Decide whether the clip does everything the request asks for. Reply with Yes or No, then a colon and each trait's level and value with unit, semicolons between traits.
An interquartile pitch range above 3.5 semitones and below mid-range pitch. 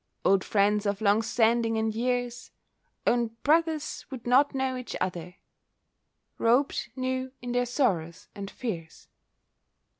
No: average, 4.0 semitones; high, 235 Hz